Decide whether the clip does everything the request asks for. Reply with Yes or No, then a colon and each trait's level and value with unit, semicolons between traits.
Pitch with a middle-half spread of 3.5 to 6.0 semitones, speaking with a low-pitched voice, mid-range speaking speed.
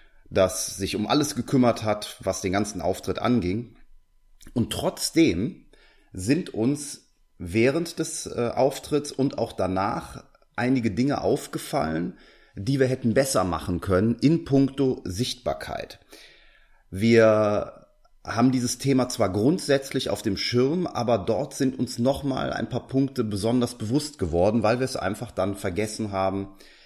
Yes: average, 5.3 semitones; low, 115 Hz; average, 135 wpm